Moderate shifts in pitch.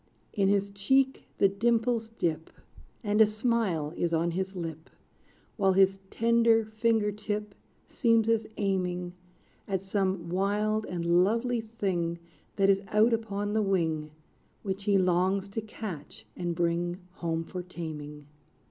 Yes: average, 3.8 semitones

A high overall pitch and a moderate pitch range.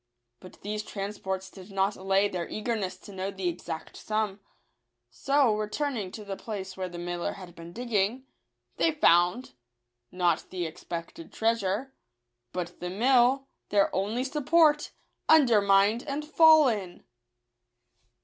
Yes: high, 200 Hz; average, 4.8 semitones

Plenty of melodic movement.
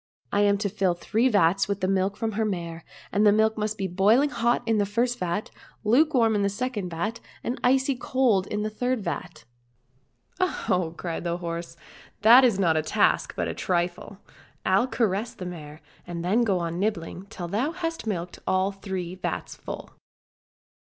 No: average, 4.3 semitones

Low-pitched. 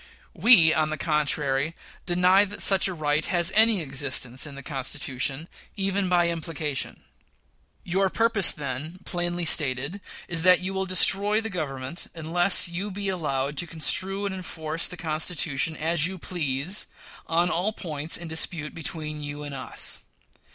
No: medium, 165 Hz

